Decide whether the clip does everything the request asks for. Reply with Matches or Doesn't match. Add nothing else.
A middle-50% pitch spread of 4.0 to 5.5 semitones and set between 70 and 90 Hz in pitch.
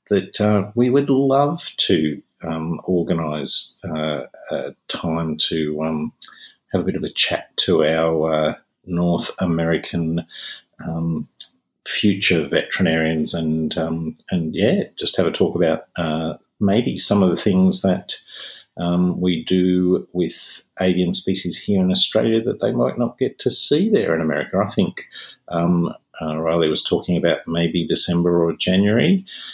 Doesn't match